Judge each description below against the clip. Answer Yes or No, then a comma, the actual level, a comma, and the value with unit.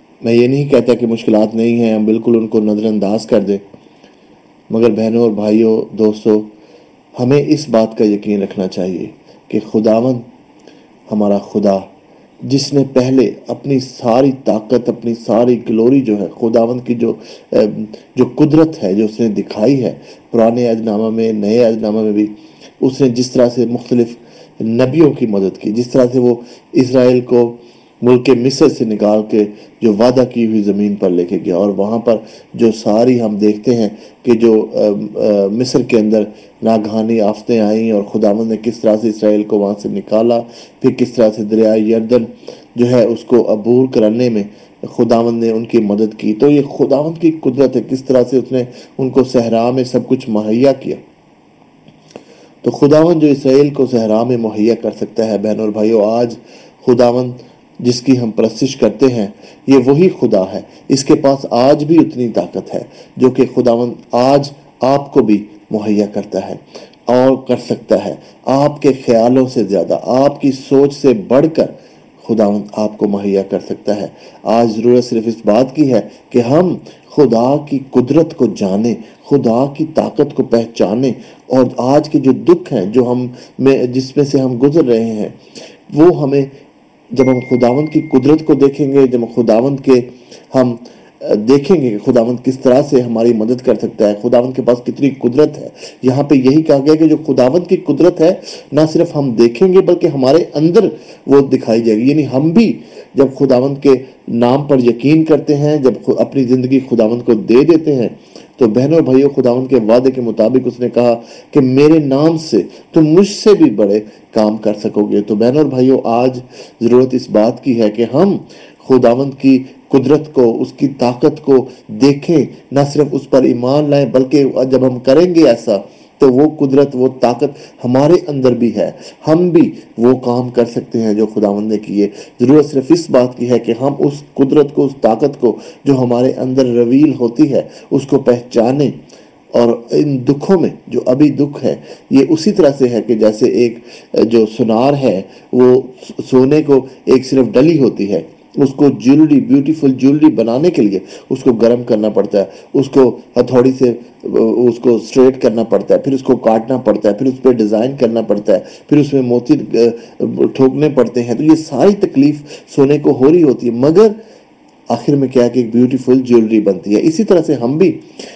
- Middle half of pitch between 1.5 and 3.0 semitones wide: No, average, 3.5 semitones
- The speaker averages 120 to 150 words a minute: No, average, 190 wpm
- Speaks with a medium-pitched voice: No, low, 125 Hz